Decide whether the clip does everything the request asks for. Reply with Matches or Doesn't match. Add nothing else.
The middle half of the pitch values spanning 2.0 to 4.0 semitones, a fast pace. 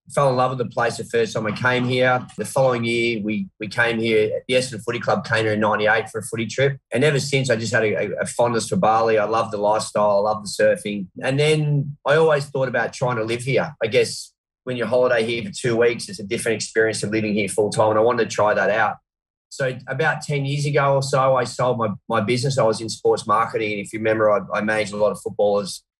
Matches